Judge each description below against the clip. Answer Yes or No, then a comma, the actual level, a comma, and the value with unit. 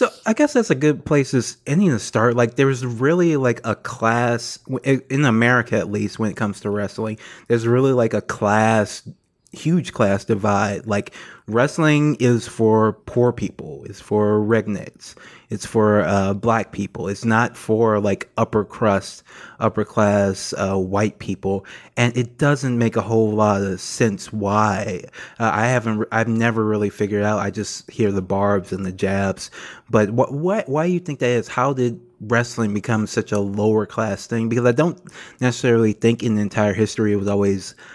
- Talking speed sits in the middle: Yes, average, 180 wpm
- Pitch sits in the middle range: No, low, 110 Hz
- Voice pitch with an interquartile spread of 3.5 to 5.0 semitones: No, average, 3.0 semitones